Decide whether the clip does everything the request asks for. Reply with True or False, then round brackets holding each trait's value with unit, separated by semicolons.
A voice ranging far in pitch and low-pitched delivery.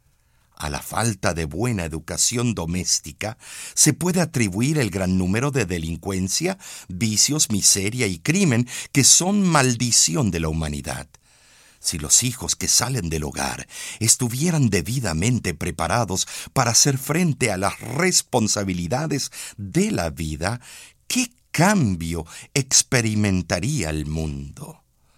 True (7.3 semitones; 110 Hz)